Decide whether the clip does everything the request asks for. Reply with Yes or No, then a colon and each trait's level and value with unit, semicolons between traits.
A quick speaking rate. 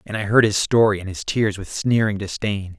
Yes: fast, 235 wpm